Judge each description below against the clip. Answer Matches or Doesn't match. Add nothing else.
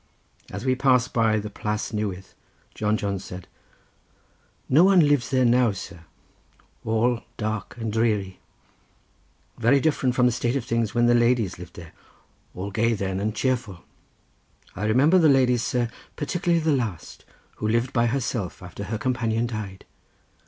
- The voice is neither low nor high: Doesn't match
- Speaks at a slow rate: Doesn't match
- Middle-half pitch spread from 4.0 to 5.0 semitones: Doesn't match